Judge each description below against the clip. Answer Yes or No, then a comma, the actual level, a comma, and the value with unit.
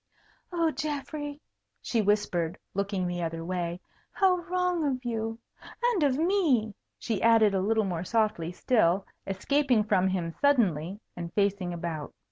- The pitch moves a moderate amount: No, wide, 7.7 semitones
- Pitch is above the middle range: Yes, high, 210 Hz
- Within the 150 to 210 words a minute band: No, average, 140 wpm